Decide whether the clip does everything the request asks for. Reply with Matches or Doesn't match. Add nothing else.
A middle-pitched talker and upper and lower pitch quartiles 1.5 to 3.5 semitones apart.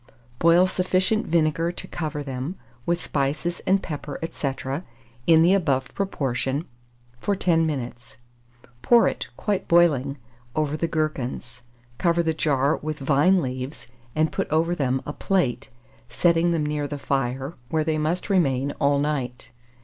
Doesn't match